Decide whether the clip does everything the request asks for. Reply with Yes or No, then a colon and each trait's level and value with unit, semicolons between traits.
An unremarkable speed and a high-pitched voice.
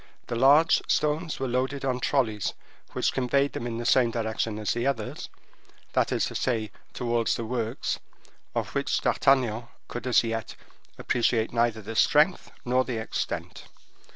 No: average, 155 wpm; low, 120 Hz